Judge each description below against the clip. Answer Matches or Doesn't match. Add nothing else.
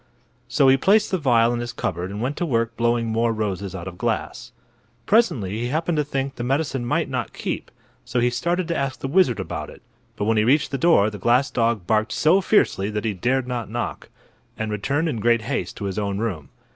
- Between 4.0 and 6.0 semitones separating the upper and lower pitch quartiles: Matches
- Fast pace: Matches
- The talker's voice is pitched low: Matches